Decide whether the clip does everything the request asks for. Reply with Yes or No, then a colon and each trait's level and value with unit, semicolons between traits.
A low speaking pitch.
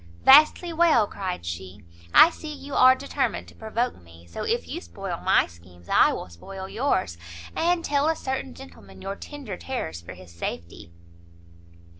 No: high, 190 Hz